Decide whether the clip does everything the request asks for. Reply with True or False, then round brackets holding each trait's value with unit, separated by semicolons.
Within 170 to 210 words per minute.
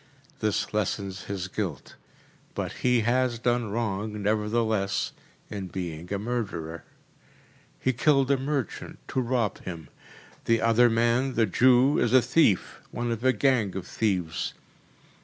False (140 wpm)